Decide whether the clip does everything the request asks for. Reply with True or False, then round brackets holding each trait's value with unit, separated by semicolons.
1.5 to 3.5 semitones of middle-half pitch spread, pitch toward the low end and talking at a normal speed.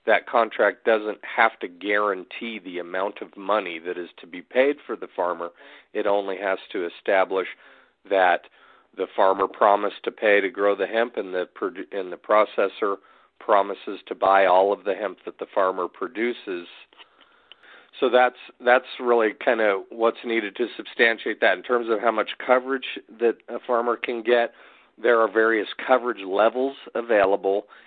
False (4.1 semitones; 110 Hz; 165 wpm)